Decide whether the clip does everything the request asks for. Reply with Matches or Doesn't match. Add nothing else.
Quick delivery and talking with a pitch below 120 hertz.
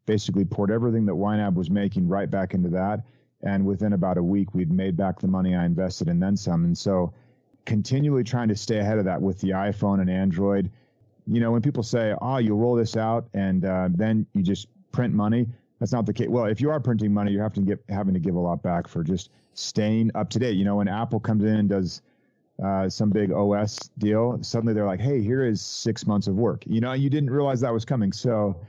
Matches